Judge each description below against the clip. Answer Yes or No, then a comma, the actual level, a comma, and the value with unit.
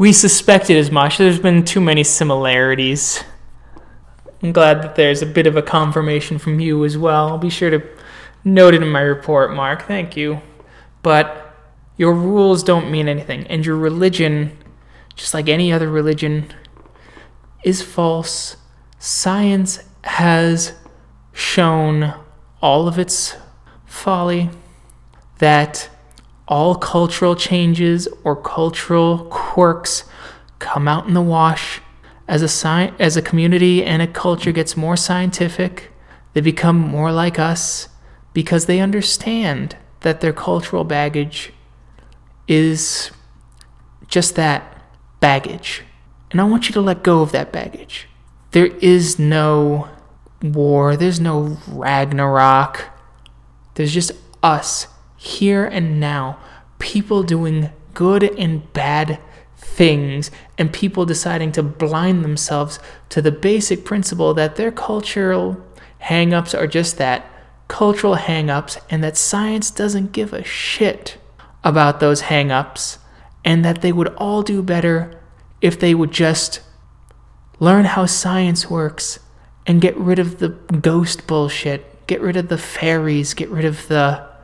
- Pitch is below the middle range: No, medium, 160 Hz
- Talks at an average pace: No, slow, 130 wpm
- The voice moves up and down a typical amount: Yes, average, 3.1 semitones